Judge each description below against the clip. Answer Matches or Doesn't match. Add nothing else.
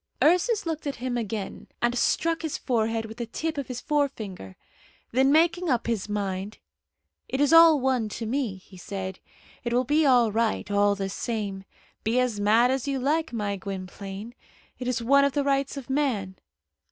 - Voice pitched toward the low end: Doesn't match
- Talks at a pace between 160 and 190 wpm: Matches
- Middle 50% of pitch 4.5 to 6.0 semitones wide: Matches